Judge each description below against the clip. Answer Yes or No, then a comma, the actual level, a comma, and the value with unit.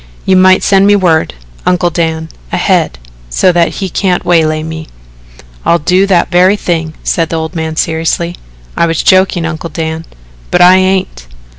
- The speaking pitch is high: No, medium, 170 Hz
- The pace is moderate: Yes, average, 165 wpm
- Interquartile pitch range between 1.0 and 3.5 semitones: Yes, narrow, 2.6 semitones